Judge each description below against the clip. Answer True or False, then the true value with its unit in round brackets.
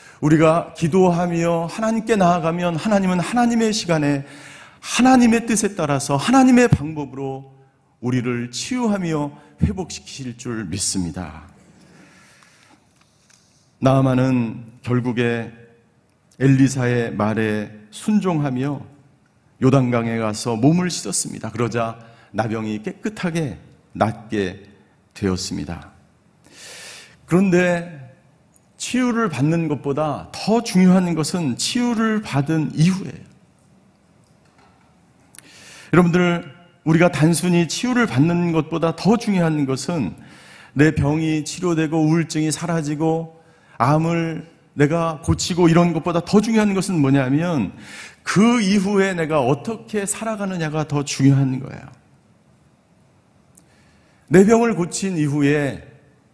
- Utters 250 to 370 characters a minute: False (235 characters per minute)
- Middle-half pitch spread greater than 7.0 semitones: False (5.1 semitones)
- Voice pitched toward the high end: False (155 Hz)